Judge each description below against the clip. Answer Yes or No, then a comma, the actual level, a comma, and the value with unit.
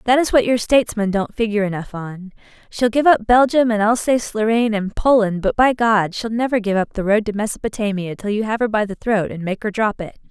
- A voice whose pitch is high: Yes, high, 220 Hz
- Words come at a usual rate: No, fast, 240 wpm